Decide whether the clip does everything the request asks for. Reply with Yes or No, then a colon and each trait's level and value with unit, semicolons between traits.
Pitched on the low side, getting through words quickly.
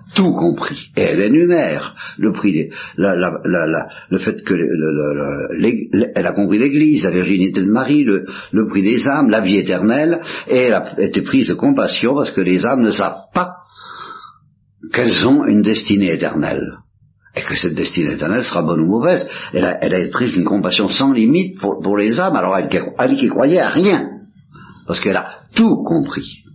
No: low, 110 Hz; average, 195 wpm